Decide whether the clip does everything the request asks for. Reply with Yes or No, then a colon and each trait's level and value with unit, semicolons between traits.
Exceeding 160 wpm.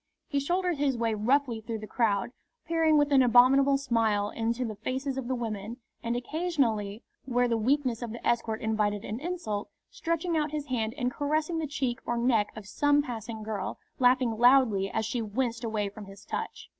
Yes: average, 190 wpm